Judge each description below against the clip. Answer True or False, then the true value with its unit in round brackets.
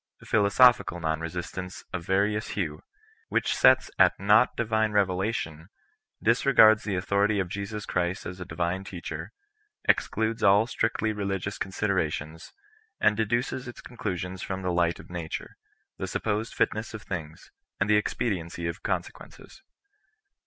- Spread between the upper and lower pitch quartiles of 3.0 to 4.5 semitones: True (3.5 semitones)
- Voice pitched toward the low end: True (100 Hz)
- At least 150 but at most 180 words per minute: False (140 wpm)